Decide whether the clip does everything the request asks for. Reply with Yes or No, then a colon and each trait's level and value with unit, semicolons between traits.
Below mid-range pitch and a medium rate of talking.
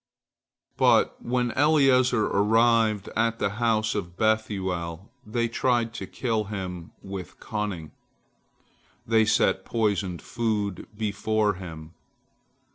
No: low, 110 Hz; slow, 110 wpm